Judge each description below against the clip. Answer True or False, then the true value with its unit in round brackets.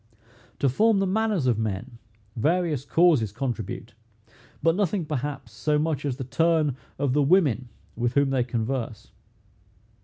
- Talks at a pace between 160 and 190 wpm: False (145 wpm)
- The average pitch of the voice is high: False (140 Hz)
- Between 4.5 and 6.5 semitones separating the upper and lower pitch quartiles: True (5.1 semitones)